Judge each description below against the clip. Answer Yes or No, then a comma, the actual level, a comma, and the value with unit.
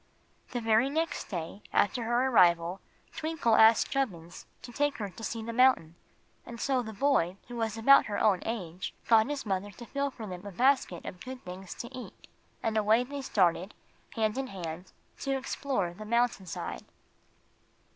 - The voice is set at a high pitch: Yes, high, 225 Hz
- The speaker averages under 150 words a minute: No, average, 175 wpm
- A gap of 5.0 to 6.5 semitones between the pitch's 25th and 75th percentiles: Yes, average, 5.3 semitones